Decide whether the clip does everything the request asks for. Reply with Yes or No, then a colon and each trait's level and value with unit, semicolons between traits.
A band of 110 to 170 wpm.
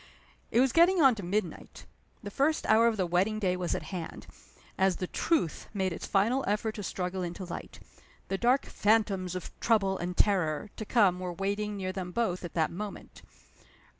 No: average, 190 wpm